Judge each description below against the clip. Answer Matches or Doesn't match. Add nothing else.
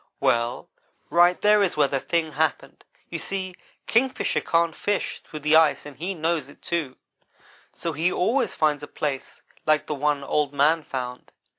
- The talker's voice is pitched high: Doesn't match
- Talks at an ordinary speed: Matches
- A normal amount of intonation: Matches